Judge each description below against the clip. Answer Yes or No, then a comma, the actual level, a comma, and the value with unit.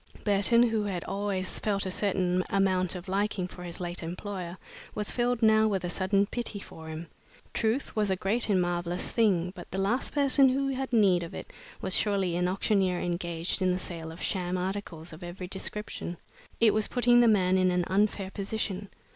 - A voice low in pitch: No, high, 190 Hz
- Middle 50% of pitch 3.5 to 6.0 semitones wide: No, average, 3.0 semitones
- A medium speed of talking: Yes, average, 195 wpm